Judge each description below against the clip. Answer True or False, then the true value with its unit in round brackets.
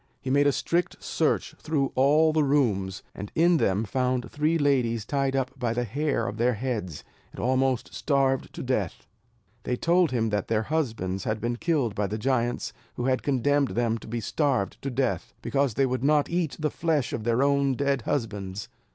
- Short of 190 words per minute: False (195 wpm)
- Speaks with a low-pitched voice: True (130 Hz)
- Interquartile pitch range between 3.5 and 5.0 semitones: True (4.0 semitones)